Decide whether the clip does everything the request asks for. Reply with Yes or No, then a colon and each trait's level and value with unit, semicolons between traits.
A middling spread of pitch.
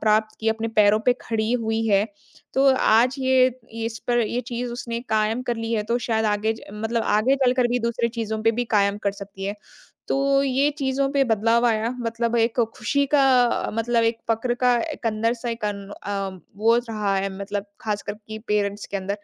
No: narrow, 2.2 semitones